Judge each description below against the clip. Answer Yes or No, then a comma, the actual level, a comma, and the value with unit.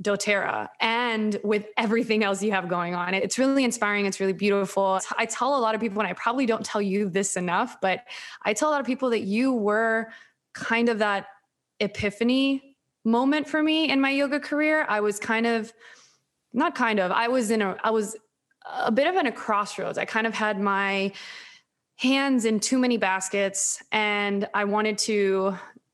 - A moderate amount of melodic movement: Yes, average, 3.4 semitones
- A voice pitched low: No, high, 220 Hz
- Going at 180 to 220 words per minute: Yes, average, 190 wpm